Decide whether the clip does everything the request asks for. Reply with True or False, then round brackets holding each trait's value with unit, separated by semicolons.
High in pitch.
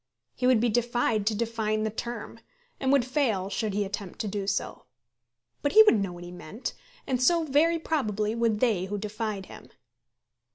True (220 Hz)